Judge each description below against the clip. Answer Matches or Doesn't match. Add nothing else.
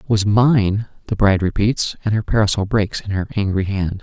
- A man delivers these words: Matches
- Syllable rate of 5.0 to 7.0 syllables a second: Matches